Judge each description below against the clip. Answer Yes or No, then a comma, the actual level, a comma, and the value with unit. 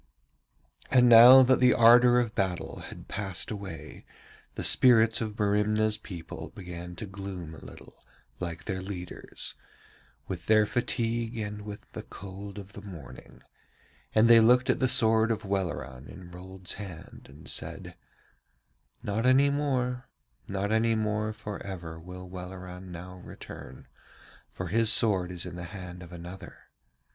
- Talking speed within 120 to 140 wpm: No, average, 150 wpm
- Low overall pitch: Yes, low, 100 Hz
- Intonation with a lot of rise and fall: No, average, 3.9 semitones